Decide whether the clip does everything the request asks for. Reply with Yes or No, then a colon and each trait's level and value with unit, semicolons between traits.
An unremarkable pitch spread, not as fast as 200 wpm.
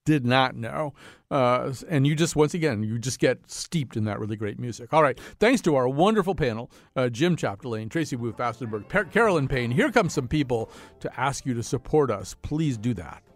No: average, 5.0 semitones; fast, 205 wpm